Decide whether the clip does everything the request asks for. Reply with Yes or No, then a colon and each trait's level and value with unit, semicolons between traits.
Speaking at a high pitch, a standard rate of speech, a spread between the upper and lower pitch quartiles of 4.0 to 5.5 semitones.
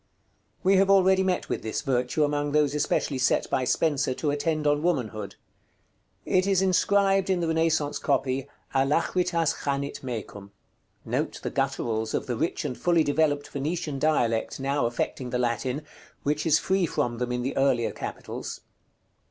No: medium, 145 Hz; average, 160 wpm; average, 4.6 semitones